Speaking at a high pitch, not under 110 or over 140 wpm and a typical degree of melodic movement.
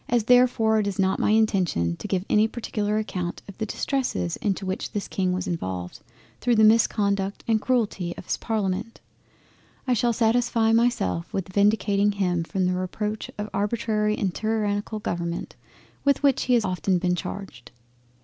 No: high, 205 Hz; average, 170 wpm; average, 3.2 semitones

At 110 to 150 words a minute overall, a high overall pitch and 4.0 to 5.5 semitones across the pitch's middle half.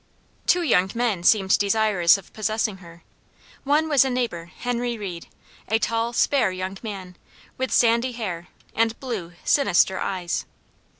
Yes: average, 140 wpm; high, 215 Hz; average, 4.5 semitones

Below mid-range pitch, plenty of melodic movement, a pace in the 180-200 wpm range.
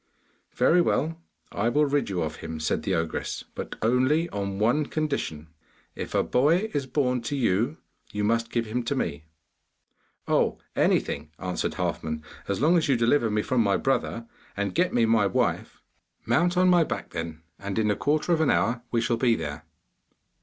Yes: low, 115 Hz; wide, 6.6 semitones; average, 185 wpm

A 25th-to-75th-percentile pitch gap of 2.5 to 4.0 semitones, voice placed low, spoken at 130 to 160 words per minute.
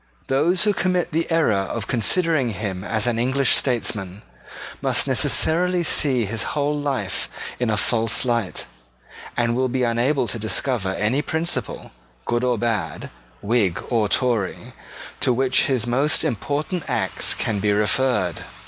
No: average, 4.7 semitones; low, 120 Hz; average, 145 wpm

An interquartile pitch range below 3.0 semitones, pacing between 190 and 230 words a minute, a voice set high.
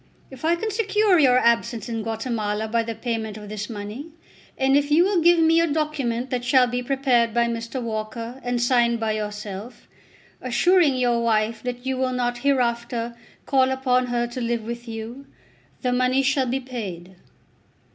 No: narrow, 2.6 semitones; average, 175 wpm; high, 245 Hz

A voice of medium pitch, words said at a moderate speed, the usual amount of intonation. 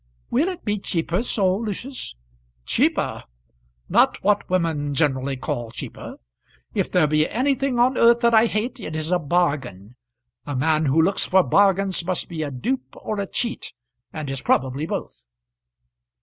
No: medium, 180 Hz; average, 160 wpm; wide, 7.1 semitones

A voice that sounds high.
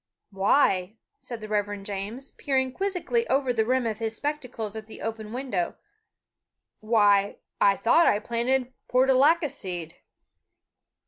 Yes: high, 225 Hz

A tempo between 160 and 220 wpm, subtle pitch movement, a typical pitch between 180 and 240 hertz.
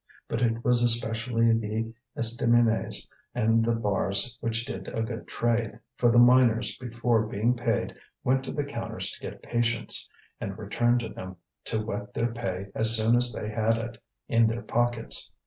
No: average, 170 wpm; narrow, 1.3 semitones; low, 115 Hz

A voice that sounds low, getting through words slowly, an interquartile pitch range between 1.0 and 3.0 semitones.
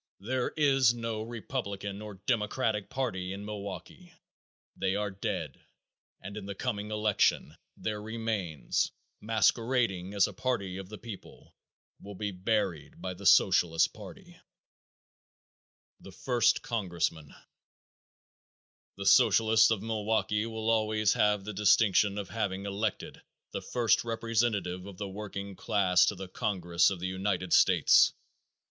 Yes: low, 105 Hz; slow, 130 wpm; average, 2.7 semitones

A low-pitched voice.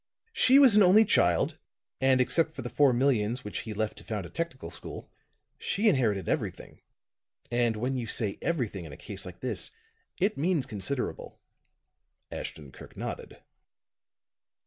Yes: low, 125 Hz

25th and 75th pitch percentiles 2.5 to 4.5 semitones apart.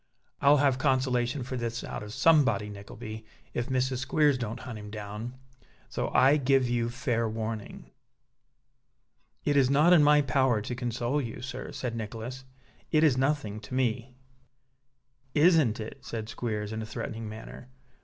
Yes: average, 3.3 semitones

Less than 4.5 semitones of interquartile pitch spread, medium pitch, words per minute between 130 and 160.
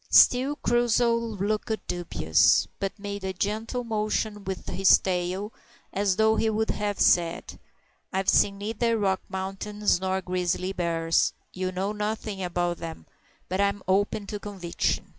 No: narrow, 2.6 semitones; high, 200 Hz; average, 140 wpm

